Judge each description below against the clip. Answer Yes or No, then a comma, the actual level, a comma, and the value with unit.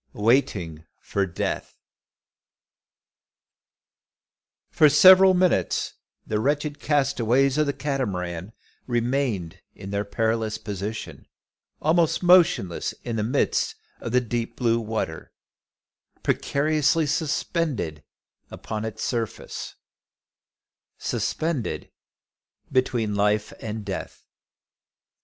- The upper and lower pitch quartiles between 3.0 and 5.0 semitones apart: No, wide, 5.6 semitones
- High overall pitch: No, low, 120 Hz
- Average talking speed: No, slow, 90 wpm